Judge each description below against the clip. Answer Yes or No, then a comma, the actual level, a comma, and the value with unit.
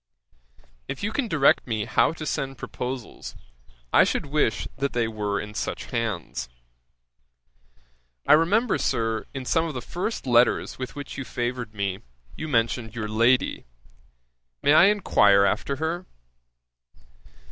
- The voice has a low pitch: Yes, low, 125 Hz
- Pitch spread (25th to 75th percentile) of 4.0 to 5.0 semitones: No, wide, 5.5 semitones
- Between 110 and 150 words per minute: Yes, average, 140 wpm